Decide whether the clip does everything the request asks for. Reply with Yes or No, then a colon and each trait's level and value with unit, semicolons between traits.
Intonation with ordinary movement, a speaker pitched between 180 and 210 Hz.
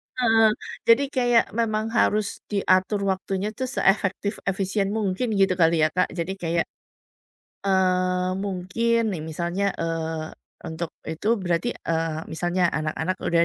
Yes: average, 3.8 semitones; high, 190 Hz